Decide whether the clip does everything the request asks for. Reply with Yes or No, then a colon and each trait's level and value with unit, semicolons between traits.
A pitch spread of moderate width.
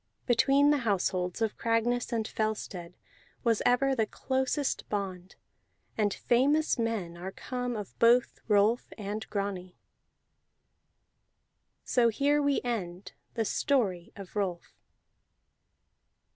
Yes: average, 4.1 semitones